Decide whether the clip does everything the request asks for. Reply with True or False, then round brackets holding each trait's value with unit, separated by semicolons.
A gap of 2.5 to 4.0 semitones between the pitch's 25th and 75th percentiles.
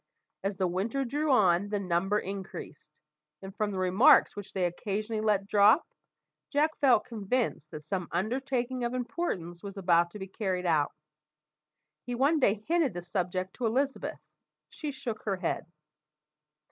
False (5.2 semitones)